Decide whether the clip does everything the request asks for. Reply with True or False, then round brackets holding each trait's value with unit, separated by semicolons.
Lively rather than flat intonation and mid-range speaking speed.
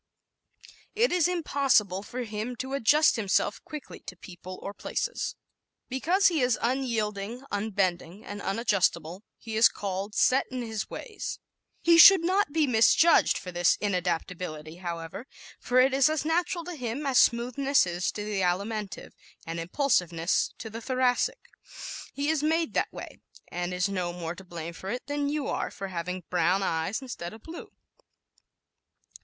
True (7.4 semitones; 160 wpm)